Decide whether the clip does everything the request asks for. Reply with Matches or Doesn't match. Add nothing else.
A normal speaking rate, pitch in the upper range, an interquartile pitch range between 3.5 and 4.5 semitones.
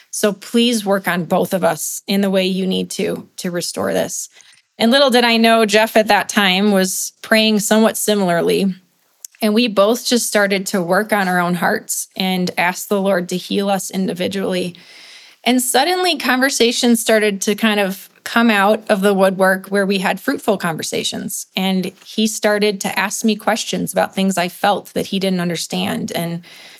Doesn't match